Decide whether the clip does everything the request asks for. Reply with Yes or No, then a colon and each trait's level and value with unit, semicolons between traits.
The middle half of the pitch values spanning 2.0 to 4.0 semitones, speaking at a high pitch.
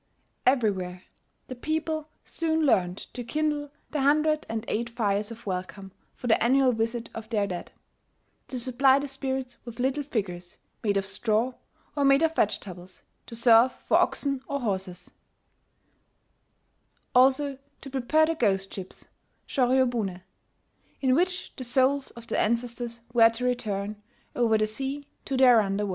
No: average, 4.5 semitones; high, 240 Hz